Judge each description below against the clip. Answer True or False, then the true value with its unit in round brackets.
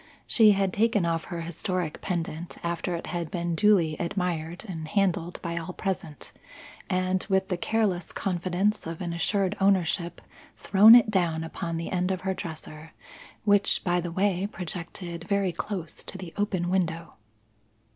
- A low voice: False (180 Hz)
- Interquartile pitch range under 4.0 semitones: True (2.4 semitones)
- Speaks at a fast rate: False (155 wpm)